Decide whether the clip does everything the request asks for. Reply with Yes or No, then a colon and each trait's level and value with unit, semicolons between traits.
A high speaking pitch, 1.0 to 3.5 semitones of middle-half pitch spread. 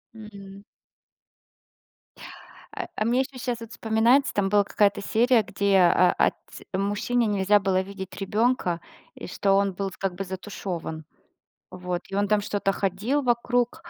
Yes: high, 200 Hz; average, 3.0 semitones